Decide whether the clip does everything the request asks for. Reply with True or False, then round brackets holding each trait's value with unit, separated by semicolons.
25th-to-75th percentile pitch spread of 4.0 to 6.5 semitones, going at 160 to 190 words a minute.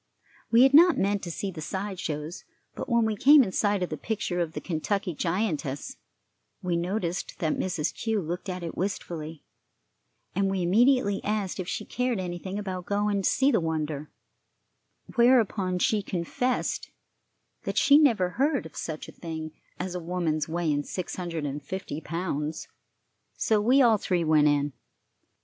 True (4.4 semitones; 170 wpm)